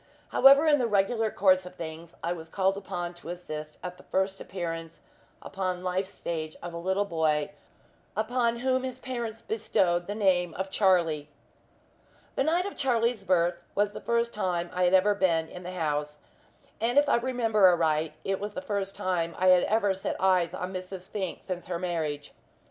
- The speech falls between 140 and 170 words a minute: No, average, 185 wpm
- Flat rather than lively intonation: No, average, 3.7 semitones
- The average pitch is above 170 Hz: Yes, medium, 185 Hz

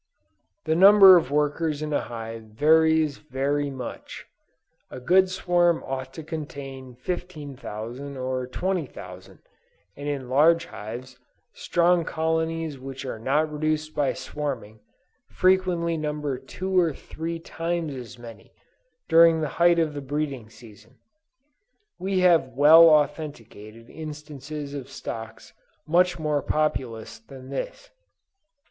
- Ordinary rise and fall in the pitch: Yes, average, 4.0 semitones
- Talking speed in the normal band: No, slow, 120 wpm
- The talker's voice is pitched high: No, medium, 150 Hz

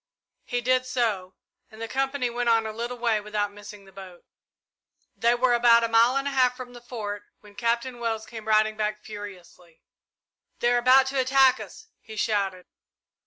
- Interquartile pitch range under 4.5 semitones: Yes, average, 2.8 semitones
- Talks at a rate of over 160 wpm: Yes, average, 185 wpm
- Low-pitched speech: No, high, 230 Hz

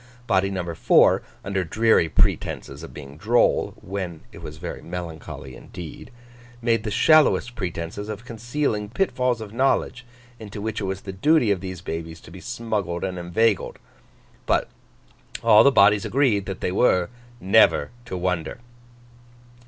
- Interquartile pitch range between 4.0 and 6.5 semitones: Yes, average, 4.5 semitones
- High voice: No, low, 100 Hz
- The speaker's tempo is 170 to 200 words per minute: No, average, 150 wpm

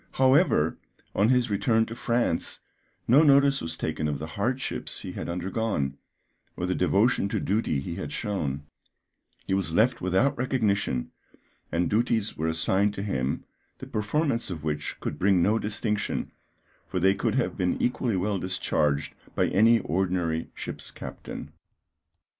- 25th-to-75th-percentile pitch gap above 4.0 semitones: Yes, wide, 5.6 semitones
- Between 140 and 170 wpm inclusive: Yes, average, 150 wpm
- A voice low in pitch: Yes, low, 100 Hz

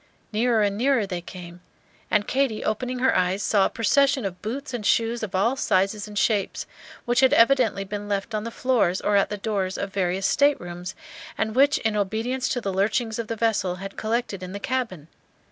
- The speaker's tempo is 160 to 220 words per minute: Yes, average, 200 wpm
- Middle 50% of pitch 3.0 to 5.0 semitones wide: Yes, average, 3.7 semitones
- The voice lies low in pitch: No, high, 215 Hz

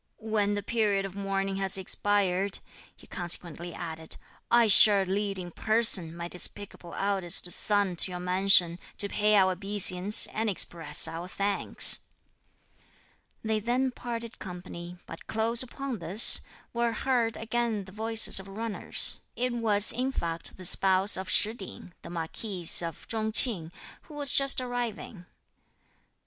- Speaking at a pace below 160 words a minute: Yes, average, 145 wpm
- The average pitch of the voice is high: Yes, high, 200 Hz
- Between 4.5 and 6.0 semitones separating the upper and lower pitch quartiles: No, average, 3.7 semitones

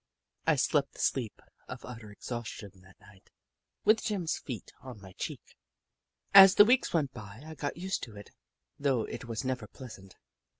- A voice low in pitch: Yes, low, 125 Hz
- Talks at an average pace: Yes, average, 175 wpm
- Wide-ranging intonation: Yes, wide, 7.2 semitones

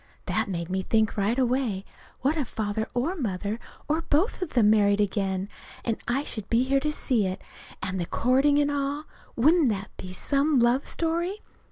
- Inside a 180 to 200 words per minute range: Yes, average, 185 wpm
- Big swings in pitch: Yes, wide, 6.0 semitones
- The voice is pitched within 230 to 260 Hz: Yes, high, 240 Hz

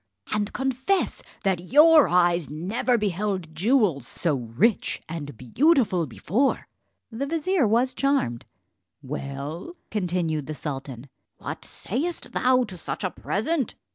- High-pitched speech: Yes, high, 195 Hz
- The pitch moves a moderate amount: No, wide, 8.9 semitones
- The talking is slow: Yes, slow, 120 wpm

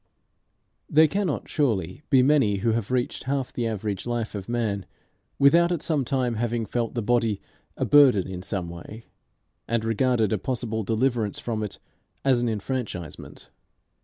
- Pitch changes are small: No, average, 3.7 semitones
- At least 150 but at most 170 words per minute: Yes, average, 160 wpm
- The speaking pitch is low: Yes, low, 115 Hz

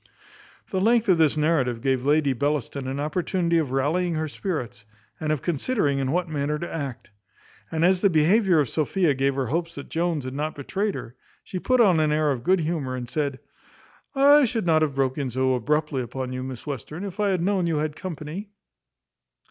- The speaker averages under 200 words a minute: No, fast, 205 wpm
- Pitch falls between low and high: Yes, medium, 155 Hz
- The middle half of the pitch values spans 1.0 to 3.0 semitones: No, average, 4.6 semitones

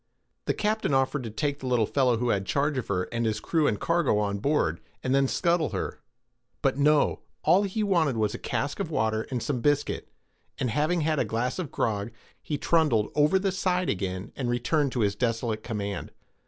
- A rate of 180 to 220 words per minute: Yes, average, 200 wpm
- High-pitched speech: No, low, 130 Hz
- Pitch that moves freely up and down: Yes, wide, 5.7 semitones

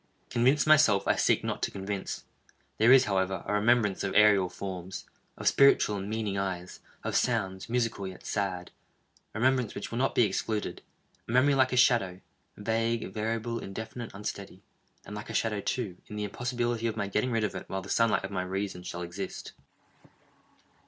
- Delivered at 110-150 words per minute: No, average, 170 wpm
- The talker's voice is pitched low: Yes, low, 105 Hz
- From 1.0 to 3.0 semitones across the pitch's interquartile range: No, average, 3.4 semitones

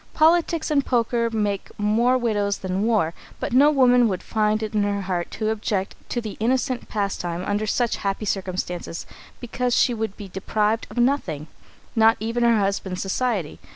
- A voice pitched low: No, high, 215 Hz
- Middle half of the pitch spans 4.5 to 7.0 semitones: No, average, 3.4 semitones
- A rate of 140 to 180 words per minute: Yes, average, 170 wpm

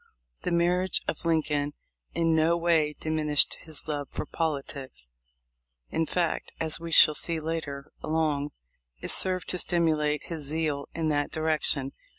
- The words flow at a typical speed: Yes, average, 150 wpm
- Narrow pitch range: Yes, narrow, 2.0 semitones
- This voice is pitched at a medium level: Yes, medium, 155 Hz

